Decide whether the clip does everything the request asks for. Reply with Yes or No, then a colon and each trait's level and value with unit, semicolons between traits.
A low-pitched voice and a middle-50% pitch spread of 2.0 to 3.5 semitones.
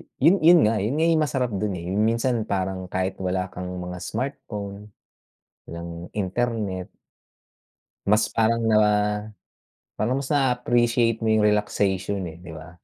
No: low, 105 Hz; average, 4.3 semitones